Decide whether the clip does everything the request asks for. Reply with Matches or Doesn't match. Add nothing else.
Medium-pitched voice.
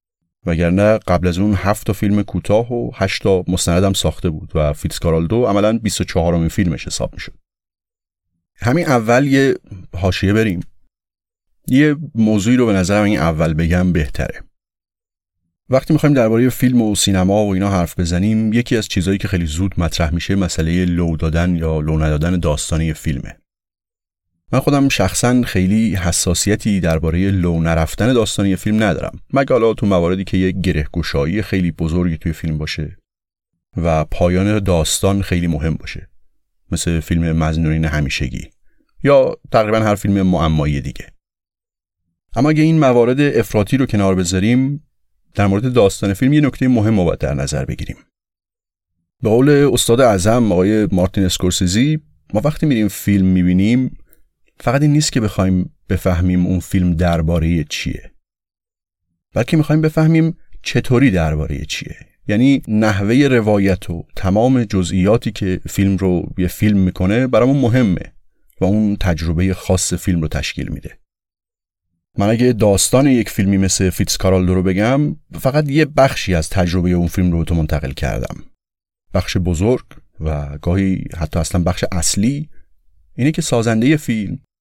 Doesn't match